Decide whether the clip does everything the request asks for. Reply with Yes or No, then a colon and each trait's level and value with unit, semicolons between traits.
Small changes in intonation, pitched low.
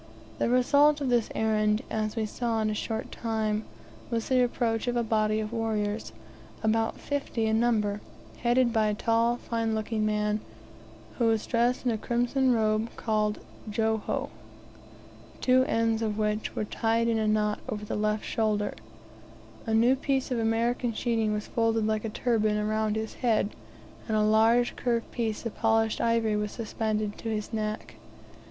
No: narrow, 1.6 semitones; high, 225 Hz